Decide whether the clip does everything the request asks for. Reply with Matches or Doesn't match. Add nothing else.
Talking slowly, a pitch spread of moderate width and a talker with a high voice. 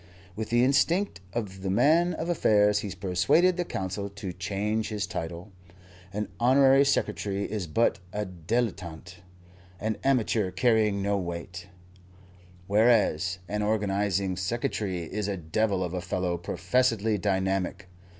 Doesn't match